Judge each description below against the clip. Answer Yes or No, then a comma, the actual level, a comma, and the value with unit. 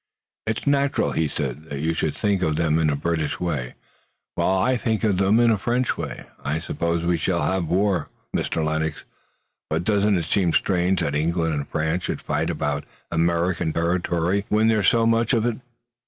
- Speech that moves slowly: No, average, 190 wpm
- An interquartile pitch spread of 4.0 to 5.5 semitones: Yes, average, 4.6 semitones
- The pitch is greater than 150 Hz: No, very low, 85 Hz